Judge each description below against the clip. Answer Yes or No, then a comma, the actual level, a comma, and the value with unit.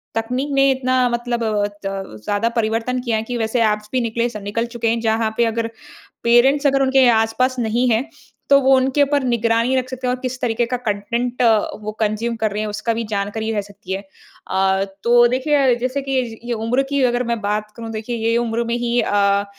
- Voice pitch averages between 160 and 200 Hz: No, high, 235 Hz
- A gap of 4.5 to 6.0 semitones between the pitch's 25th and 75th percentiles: No, narrow, 2.6 semitones